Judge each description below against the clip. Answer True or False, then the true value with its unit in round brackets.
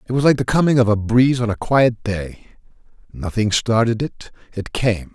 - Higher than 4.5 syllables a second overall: True (5.2 syllables/s)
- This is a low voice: True (115 Hz)